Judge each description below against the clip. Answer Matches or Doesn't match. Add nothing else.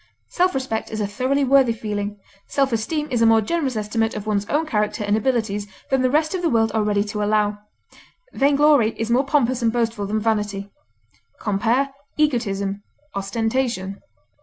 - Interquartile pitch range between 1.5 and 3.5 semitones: Doesn't match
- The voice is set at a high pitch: Matches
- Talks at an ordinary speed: Matches